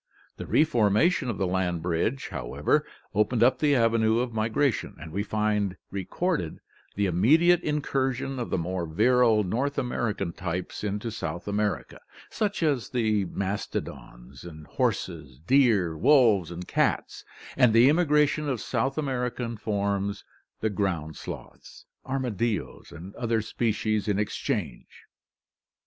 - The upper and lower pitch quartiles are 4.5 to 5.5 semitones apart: Yes, average, 5.2 semitones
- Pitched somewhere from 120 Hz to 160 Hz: No, low, 110 Hz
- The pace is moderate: No, slow, 130 wpm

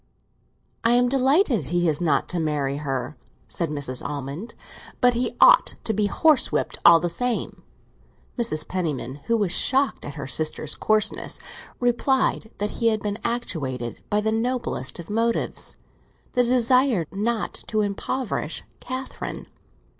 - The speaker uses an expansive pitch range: Yes, wide, 7.8 semitones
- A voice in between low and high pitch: No, high, 210 Hz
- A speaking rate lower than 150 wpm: Yes, average, 140 wpm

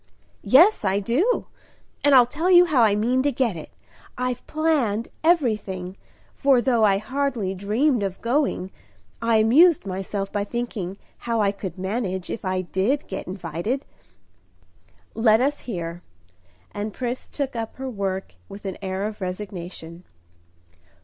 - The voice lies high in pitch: Yes, high, 215 Hz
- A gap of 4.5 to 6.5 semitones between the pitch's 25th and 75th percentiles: Yes, average, 5.1 semitones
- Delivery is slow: No, average, 145 wpm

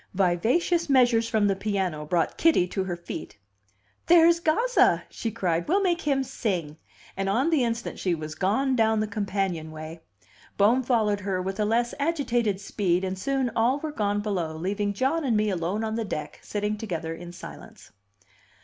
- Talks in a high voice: Yes, high, 210 Hz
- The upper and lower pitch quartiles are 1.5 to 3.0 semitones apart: No, wide, 5.4 semitones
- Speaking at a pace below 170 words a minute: No, average, 175 wpm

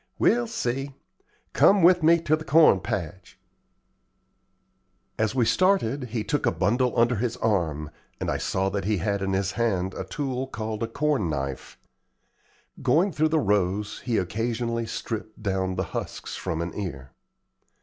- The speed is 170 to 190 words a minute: No, average, 160 wpm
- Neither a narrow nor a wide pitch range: No, wide, 5.9 semitones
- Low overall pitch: Yes, low, 110 Hz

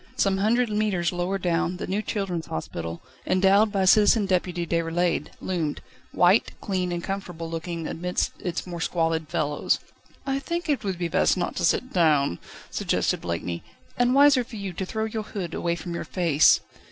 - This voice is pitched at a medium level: Yes, medium, 180 Hz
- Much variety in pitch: No, average, 3.5 semitones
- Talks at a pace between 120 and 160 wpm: No, average, 175 wpm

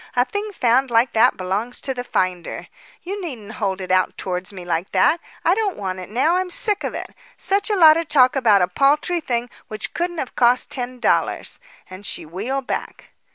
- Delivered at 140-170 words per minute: No, fast, 205 wpm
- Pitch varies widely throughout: Yes, wide, 8.8 semitones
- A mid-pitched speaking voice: No, high, 245 Hz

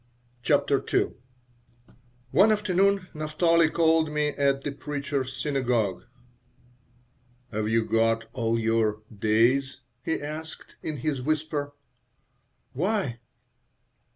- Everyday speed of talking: No, slow, 100 wpm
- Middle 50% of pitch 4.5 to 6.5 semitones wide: Yes, average, 5.1 semitones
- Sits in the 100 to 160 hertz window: Yes, medium, 140 Hz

